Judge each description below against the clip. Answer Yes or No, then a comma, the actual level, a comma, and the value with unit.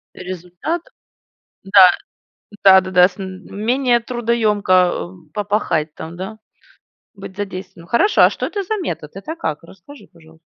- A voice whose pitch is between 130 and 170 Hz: No, high, 190 Hz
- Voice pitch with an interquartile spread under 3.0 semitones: No, average, 4.1 semitones